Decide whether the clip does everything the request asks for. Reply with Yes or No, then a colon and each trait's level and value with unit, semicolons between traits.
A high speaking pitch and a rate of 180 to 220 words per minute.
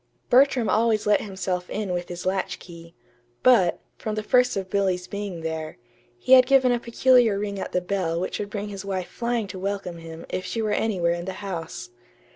Yes: high, 195 Hz; average, 200 wpm